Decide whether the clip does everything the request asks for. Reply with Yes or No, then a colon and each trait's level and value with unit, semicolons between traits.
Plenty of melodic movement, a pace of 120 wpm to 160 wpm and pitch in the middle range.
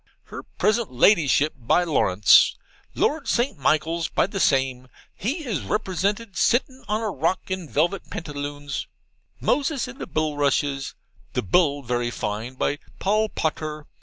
Yes: wide, 7.0 semitones; slow, 135 wpm; medium, 160 Hz